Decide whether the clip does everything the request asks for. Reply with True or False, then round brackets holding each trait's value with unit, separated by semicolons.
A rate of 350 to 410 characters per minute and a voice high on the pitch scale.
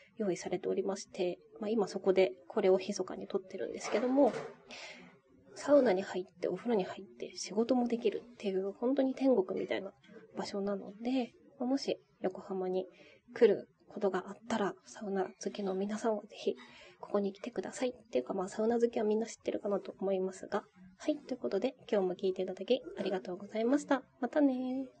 True (400 characters per minute; 200 Hz)